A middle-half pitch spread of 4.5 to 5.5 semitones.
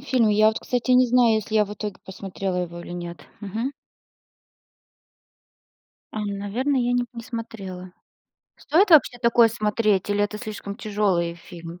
No: average, 3.8 semitones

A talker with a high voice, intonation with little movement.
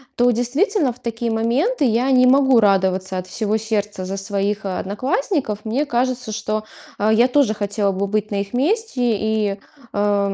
No: high, 220 Hz; average, 3.7 semitones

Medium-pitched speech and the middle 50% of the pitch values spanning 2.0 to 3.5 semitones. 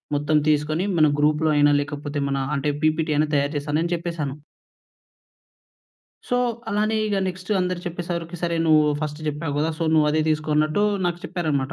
Yes: medium, 155 Hz; narrow, 2.4 semitones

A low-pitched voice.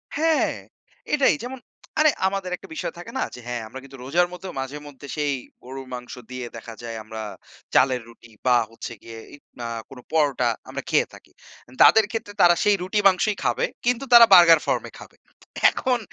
No: medium, 150 Hz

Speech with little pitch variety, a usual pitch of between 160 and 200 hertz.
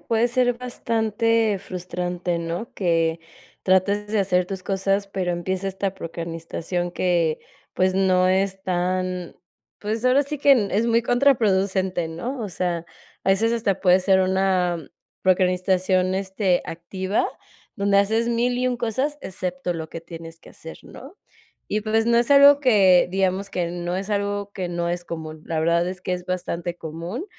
No: average, 3.3 semitones; high, 190 Hz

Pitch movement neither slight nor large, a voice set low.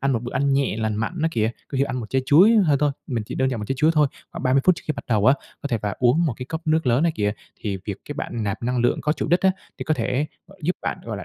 Yes: average, 4.7 semitones; low, 130 Hz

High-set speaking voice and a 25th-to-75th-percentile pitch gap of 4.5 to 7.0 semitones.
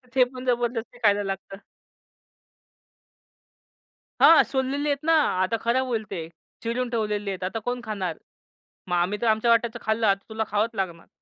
No: high, 225 Hz; average, 3.6 semitones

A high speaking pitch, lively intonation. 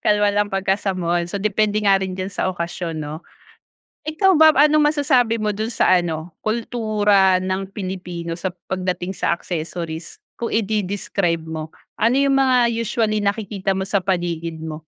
No: high, 195 Hz; average, 3.7 semitones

